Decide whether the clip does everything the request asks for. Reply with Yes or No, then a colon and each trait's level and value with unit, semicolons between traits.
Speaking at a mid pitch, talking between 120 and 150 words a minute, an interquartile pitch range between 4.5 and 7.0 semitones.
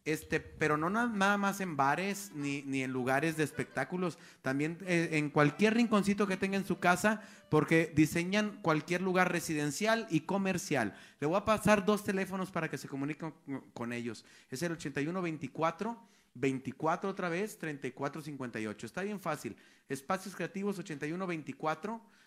Yes: medium, 165 Hz; average, 145 wpm; average, 5.2 semitones